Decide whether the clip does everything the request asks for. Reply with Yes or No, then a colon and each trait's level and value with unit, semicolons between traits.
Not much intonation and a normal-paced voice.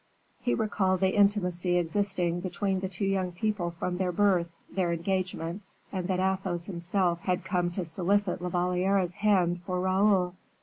Yes: narrow, 1.8 semitones; average, 160 wpm